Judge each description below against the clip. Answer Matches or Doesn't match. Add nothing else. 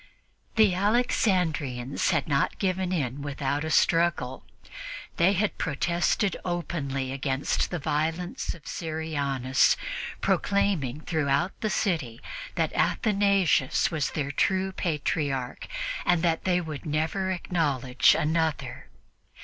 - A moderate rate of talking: Doesn't match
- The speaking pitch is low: Doesn't match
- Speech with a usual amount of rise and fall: Matches